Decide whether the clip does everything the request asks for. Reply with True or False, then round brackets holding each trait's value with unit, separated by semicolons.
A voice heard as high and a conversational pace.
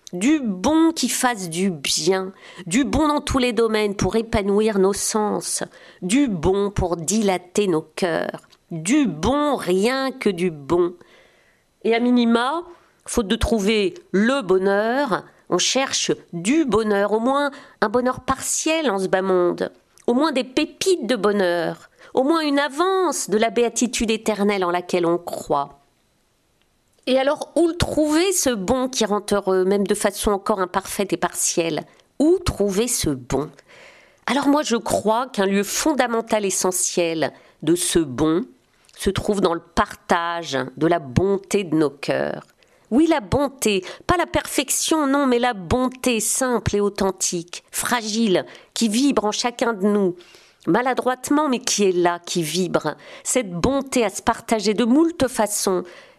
True (215 Hz; 155 wpm)